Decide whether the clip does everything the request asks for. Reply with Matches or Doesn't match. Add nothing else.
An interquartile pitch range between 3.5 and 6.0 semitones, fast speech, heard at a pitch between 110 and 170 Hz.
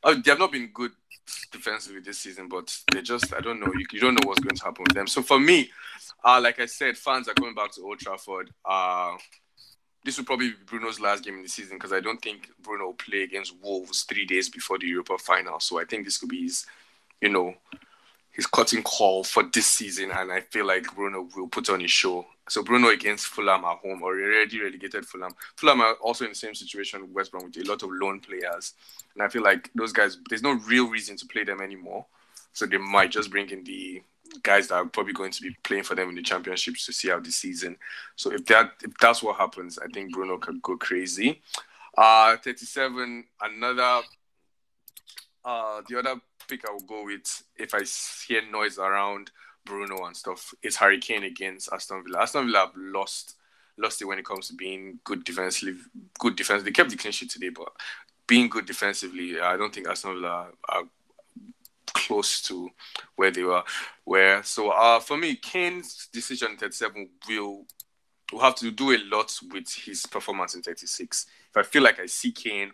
Doesn't match